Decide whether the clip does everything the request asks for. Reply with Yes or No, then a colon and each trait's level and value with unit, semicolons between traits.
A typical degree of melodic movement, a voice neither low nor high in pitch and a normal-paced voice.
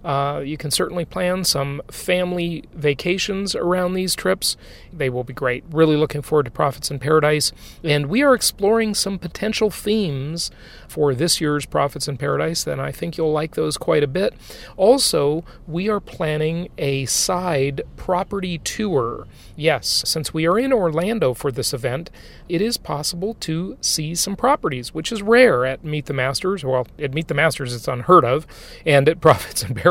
Yes: average, 4.3 semitones; medium, 160 Hz; average, 175 wpm